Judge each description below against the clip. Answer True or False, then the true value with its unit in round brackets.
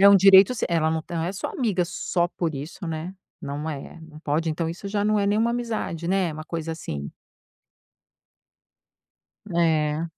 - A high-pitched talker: False (170 Hz)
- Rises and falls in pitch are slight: False (3.8 semitones)